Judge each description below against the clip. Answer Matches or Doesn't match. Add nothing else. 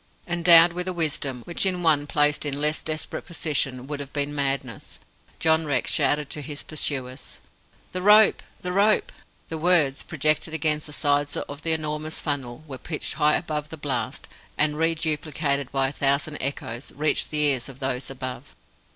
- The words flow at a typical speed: Matches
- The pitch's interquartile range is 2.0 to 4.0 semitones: Matches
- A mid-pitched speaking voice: Matches